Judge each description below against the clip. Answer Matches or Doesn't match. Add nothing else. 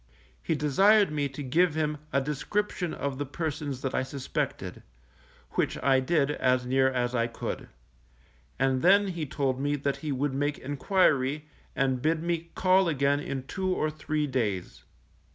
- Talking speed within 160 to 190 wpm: Matches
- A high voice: Doesn't match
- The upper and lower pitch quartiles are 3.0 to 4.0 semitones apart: Matches